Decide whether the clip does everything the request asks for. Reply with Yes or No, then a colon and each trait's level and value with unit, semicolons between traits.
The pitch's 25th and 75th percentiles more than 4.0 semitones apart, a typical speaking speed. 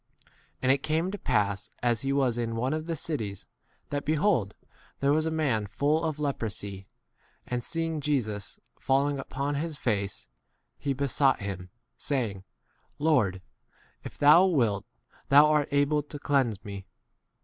Yes: wide, 5.6 semitones; average, 155 wpm